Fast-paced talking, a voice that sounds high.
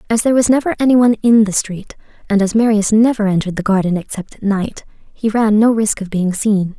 Yes: fast, 230 wpm; high, 210 Hz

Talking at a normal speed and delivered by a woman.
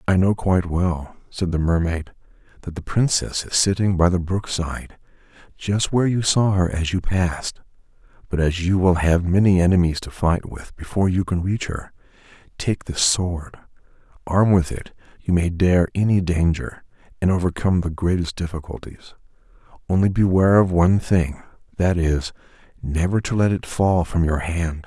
No: average, 165 wpm; male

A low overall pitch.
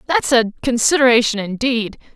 No: high, 240 Hz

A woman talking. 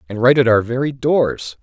No: male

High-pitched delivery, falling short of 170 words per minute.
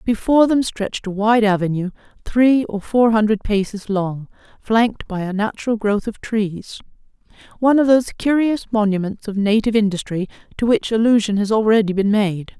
Yes: high, 215 Hz; average, 155 wpm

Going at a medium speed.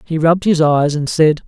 No: fast, 245 wpm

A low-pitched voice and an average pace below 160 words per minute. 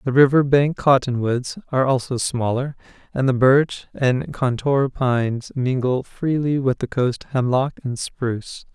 Yes: low, 130 Hz; average, 145 wpm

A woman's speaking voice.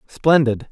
No: male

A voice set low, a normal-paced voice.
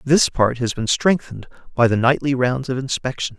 Yes: low, 130 Hz; average, 195 wpm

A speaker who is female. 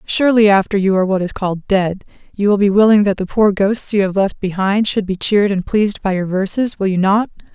Yes: female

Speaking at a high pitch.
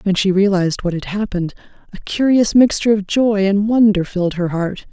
Yes: high, 200 Hz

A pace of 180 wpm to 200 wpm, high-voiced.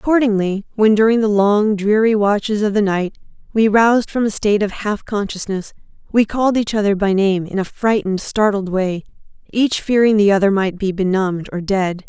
Yes: average, 190 wpm; high, 205 Hz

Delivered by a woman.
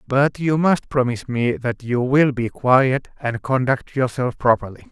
No: male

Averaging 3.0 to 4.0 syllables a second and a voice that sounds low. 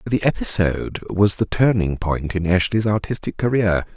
No: 4.9 syllables/s; low, 100 Hz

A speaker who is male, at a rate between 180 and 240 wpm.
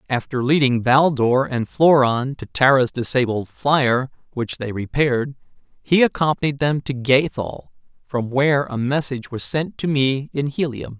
No: male; average, 155 wpm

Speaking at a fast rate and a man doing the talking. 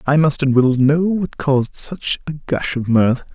Yes: fast, 215 wpm; male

